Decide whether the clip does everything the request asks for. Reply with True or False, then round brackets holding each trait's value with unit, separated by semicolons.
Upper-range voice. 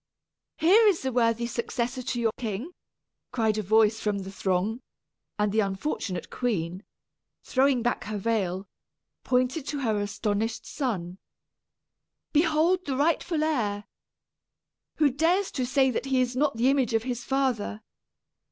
True (240 Hz)